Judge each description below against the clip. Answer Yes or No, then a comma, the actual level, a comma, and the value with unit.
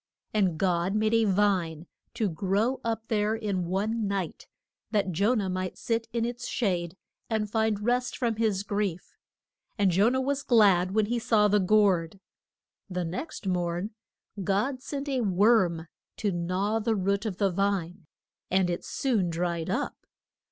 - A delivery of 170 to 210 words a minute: No, average, 160 wpm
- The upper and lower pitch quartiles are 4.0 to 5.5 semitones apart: No, average, 3.4 semitones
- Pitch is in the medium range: No, high, 205 Hz